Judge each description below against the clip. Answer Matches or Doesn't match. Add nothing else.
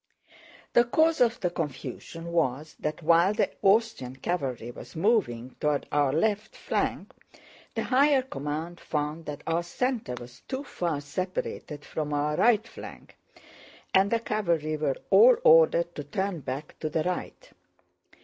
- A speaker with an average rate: Matches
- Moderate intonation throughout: Doesn't match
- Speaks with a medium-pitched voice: Matches